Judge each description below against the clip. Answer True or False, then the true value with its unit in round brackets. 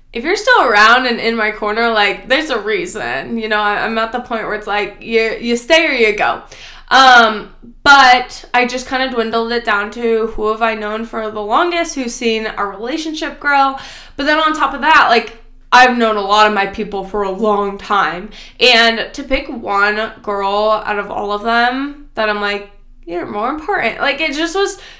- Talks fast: True (210 wpm)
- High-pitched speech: True (230 Hz)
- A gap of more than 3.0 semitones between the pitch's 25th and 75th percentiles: True (4.3 semitones)